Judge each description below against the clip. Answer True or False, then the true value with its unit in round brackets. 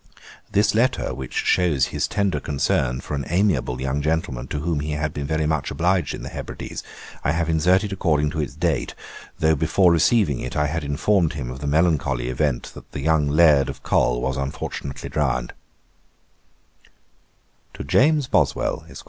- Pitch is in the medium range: False (75 Hz)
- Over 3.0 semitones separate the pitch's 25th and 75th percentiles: True (3.7 semitones)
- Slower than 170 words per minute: False (175 wpm)